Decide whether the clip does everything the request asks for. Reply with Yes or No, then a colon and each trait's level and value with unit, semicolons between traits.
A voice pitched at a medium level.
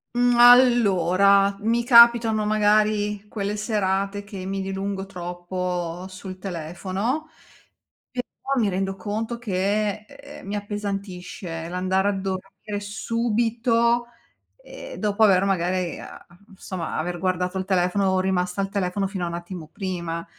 No: high, 195 Hz